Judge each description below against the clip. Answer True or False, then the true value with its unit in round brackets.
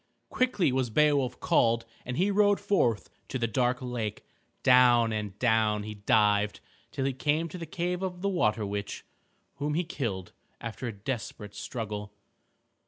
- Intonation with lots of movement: True (5.9 semitones)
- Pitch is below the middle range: True (120 Hz)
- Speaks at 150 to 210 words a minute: True (160 wpm)